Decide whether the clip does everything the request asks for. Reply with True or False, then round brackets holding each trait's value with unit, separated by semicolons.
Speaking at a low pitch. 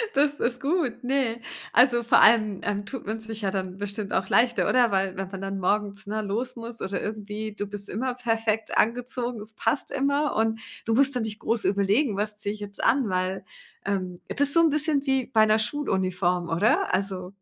False (220 Hz)